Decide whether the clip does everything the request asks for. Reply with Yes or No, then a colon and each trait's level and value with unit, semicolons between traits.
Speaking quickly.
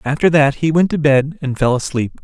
Yes: fast, 240 wpm